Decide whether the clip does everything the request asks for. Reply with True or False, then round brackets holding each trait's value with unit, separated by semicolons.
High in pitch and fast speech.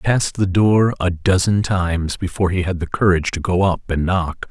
False (90 Hz; 225 wpm)